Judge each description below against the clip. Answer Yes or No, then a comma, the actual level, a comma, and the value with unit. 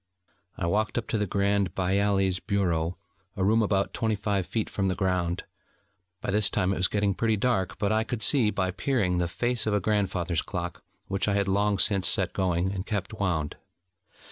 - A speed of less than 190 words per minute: No, average, 195 wpm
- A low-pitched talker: Yes, low, 100 Hz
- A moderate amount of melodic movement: No, narrow, 2.3 semitones